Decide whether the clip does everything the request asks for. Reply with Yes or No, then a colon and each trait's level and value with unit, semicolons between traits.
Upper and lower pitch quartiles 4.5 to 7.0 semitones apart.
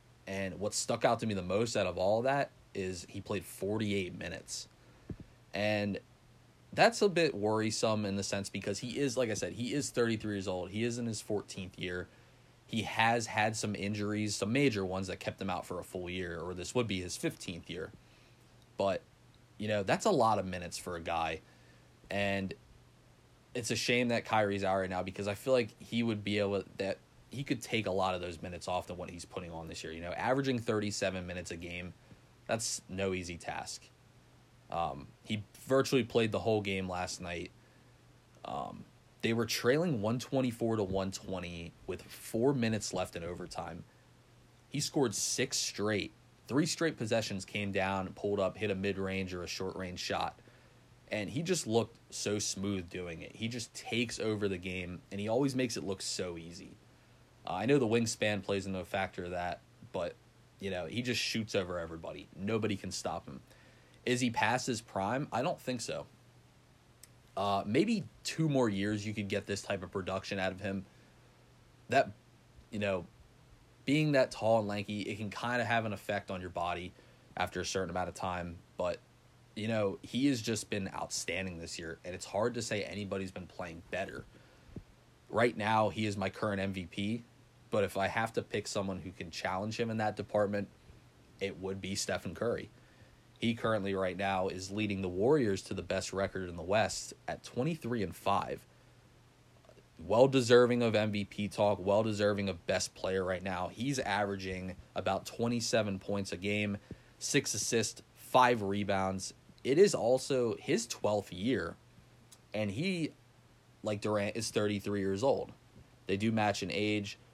No: average, 3.7 semitones